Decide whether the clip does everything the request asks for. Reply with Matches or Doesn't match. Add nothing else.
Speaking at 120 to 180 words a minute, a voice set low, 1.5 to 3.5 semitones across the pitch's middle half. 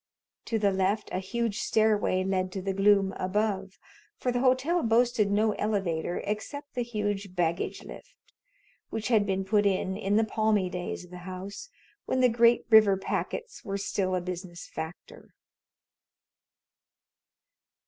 Doesn't match